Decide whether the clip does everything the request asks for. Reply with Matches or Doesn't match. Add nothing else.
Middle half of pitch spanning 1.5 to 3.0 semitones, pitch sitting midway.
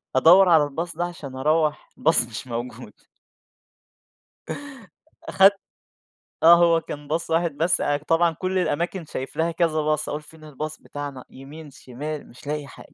Matches